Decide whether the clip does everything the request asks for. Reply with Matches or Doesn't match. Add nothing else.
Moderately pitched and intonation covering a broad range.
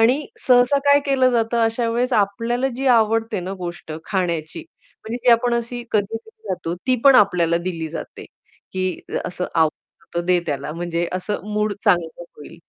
Doesn't match